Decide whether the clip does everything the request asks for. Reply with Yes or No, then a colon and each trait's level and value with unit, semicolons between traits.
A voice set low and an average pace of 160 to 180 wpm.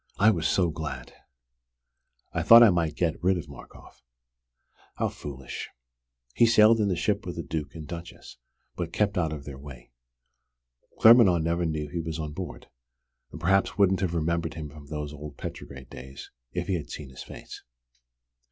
Yes: very low, 80 Hz; average, 175 wpm